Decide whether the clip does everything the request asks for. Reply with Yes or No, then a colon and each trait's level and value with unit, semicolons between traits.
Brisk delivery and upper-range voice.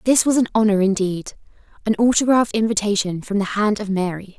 No: average, 165 wpm; high, 210 Hz